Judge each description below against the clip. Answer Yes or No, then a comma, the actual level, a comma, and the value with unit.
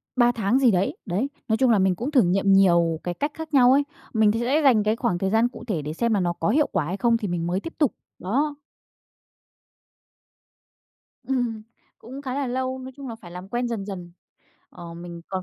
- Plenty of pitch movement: Yes, wide, 6.0 semitones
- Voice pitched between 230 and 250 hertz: No, high, 220 Hz